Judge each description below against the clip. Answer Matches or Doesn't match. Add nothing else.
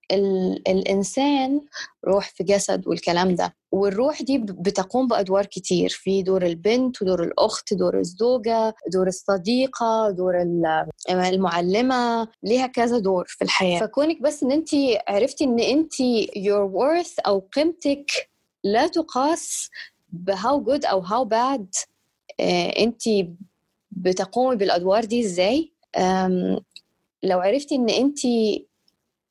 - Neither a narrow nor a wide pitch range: Doesn't match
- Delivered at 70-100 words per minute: Doesn't match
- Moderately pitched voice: Doesn't match